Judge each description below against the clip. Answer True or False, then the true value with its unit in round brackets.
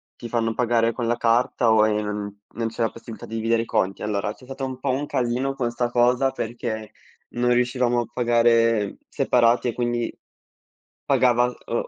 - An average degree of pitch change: False (1.4 semitones)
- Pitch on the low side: True (120 Hz)